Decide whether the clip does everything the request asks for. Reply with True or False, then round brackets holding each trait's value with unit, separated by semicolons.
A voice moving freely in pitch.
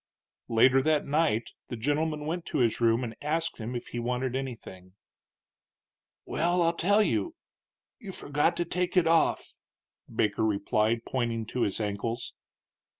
True (6.1 semitones)